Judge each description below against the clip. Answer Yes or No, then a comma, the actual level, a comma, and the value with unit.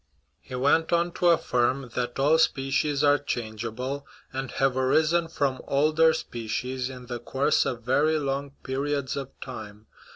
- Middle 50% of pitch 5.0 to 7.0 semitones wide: No, average, 2.7 semitones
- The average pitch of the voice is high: No, low, 135 Hz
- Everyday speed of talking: Yes, average, 150 wpm